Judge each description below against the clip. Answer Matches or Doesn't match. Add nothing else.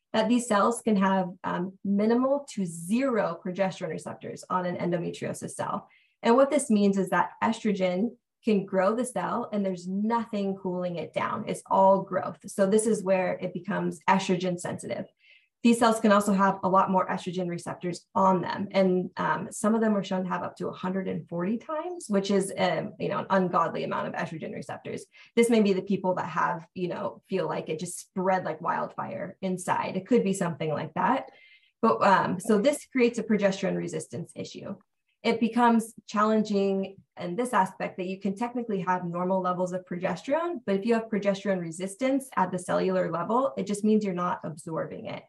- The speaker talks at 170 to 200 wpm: Matches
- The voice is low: Doesn't match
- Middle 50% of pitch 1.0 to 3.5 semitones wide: Matches